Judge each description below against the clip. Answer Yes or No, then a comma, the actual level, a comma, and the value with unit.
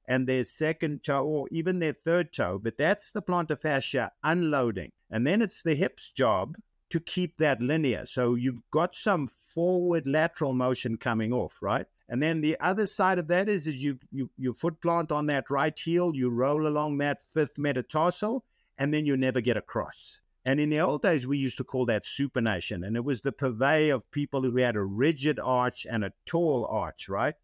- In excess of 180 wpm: Yes, fast, 205 wpm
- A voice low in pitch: No, medium, 145 Hz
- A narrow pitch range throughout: No, average, 4.4 semitones